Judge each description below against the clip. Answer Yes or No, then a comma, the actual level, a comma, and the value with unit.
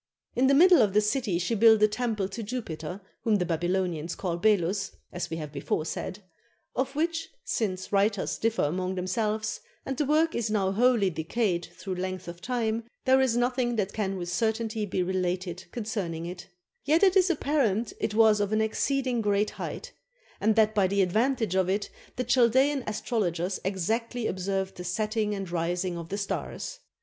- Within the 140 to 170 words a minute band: No, average, 180 wpm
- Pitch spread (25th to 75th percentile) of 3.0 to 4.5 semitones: Yes, average, 4.2 semitones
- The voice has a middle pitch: No, high, 210 Hz